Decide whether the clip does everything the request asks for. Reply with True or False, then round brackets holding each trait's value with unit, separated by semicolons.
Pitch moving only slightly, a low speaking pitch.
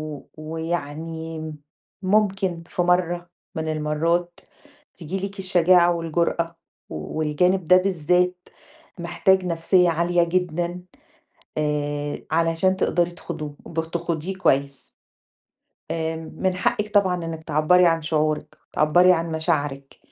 False (2.3 semitones; 170 Hz)